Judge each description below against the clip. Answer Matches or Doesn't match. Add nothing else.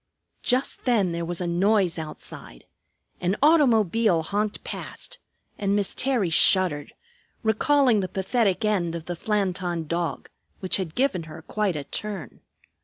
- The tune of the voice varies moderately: Matches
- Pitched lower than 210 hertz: Matches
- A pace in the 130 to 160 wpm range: Matches